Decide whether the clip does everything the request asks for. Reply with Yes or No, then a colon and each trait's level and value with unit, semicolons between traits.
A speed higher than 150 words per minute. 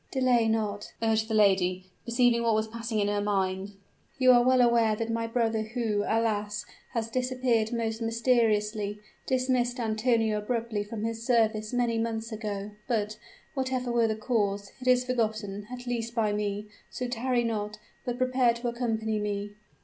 Yes: average, 165 wpm